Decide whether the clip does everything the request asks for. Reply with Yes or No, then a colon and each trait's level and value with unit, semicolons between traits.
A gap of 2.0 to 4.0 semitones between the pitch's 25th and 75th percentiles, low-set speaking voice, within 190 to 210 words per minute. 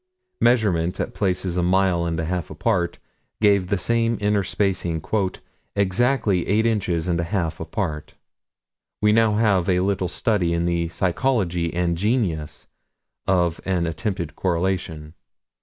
No: average, 3.5 semitones; very low, 90 Hz; average, 140 wpm